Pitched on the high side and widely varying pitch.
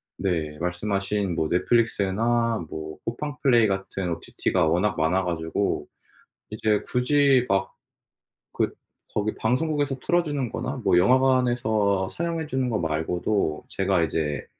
No: low, 105 Hz; wide, 5.9 semitones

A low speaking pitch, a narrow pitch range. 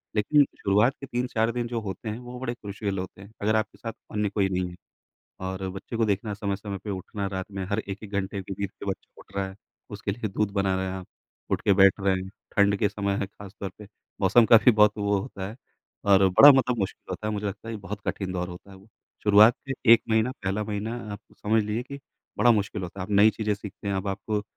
Yes: low, 100 Hz; narrow, 2.1 semitones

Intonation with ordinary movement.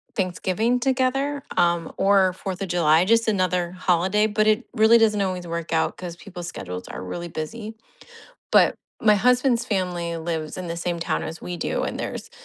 Yes: average, 4.1 semitones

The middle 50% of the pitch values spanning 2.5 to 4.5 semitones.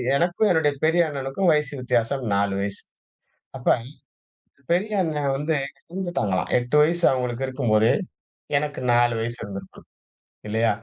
No: wide, 5.5 semitones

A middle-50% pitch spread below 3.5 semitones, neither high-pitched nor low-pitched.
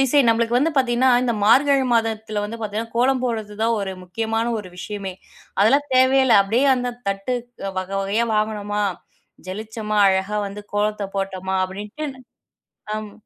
No: average, 3.1 semitones; high, 220 Hz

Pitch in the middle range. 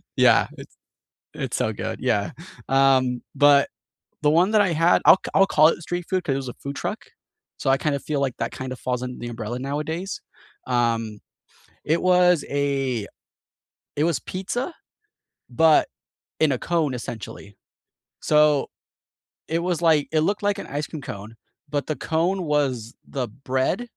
Yes: medium, 145 Hz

